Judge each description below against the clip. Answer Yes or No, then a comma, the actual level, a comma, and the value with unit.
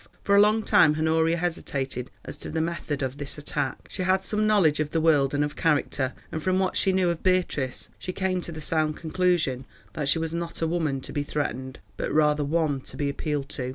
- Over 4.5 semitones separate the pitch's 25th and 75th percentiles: No, average, 3.5 semitones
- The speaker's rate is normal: No, fast, 225 wpm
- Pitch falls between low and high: Yes, medium, 160 Hz